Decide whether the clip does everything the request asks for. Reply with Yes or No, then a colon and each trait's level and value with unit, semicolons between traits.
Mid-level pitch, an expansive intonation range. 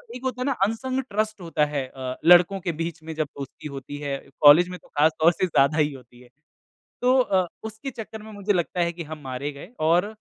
Yes: medium, 170 Hz; wide, 6.2 semitones